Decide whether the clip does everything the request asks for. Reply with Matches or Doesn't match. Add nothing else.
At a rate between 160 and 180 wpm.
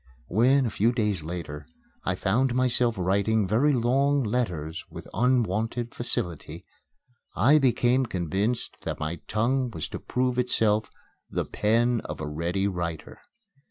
Doesn't match